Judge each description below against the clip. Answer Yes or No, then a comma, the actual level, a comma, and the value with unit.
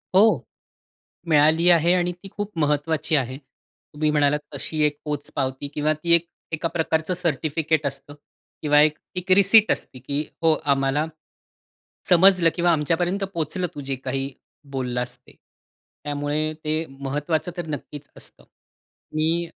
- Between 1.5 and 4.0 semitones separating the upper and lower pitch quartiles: Yes, average, 2.9 semitones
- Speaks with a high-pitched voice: No, medium, 155 Hz